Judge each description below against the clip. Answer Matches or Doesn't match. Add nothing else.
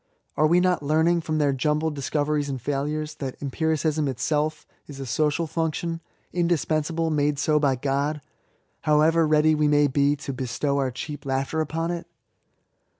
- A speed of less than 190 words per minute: Matches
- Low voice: Doesn't match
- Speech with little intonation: Matches